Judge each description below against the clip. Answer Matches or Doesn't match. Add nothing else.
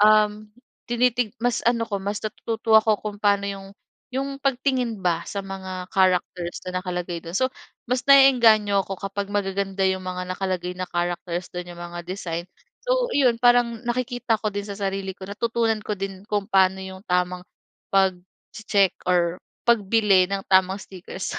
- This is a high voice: Matches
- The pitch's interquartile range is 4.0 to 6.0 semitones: Doesn't match